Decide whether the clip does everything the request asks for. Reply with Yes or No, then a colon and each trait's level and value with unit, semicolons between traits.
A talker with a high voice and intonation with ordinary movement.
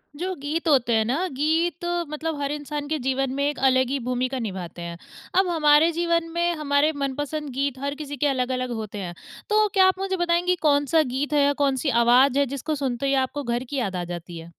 Yes: very high, 285 Hz; average, 3.7 semitones